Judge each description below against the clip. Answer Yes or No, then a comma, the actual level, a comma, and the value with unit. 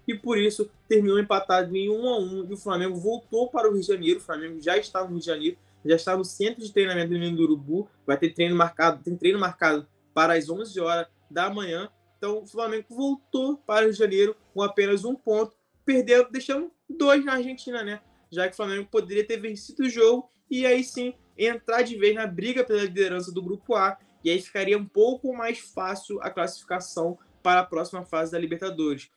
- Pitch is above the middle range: Yes, high, 200 Hz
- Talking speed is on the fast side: Yes, fast, 220 wpm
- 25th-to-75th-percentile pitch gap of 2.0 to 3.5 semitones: No, average, 4.6 semitones